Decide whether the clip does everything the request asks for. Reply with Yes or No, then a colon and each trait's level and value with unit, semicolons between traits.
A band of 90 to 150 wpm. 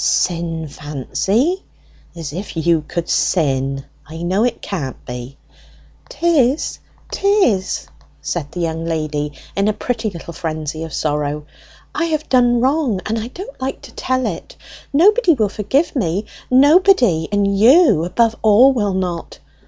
Yes: average, 145 wpm